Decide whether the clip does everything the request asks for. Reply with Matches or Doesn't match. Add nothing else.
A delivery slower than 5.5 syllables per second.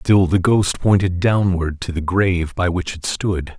Matches